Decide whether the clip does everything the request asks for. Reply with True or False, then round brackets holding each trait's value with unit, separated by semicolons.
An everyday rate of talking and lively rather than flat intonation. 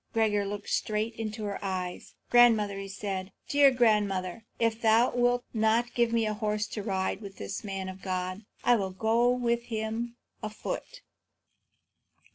False (155 wpm; 2.9 semitones)